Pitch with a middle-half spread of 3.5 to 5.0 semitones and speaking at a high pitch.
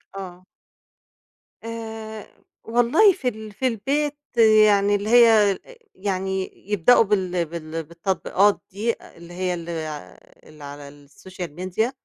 Yes: average, 4.6 semitones; high, 195 Hz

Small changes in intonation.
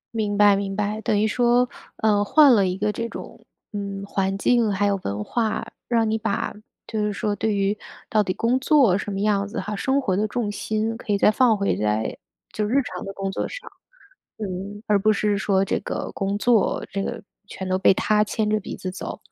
Yes: narrow, 1.9 semitones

